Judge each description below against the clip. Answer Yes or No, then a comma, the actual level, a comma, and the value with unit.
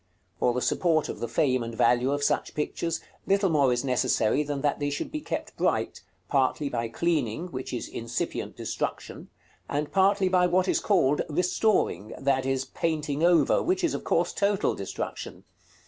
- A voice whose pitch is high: No, medium, 145 Hz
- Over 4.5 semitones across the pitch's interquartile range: Yes, wide, 5.6 semitones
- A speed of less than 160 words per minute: No, average, 175 wpm